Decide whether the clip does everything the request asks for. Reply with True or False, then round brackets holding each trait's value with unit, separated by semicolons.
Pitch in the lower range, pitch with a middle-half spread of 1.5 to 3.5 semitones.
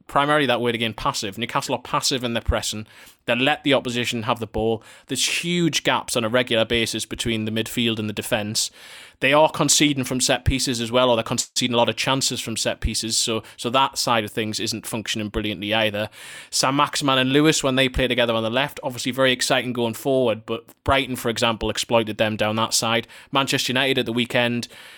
True (120 Hz; 2.9 semitones)